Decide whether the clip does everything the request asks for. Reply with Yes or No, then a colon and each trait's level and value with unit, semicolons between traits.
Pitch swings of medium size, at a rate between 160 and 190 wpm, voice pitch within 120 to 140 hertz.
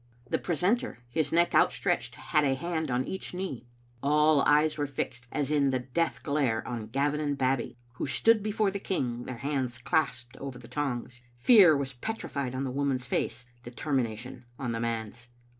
Yes: average, 3.8 semitones; average, 175 wpm; low, 135 Hz